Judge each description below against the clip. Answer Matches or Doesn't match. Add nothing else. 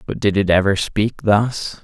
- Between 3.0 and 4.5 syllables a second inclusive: Matches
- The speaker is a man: Matches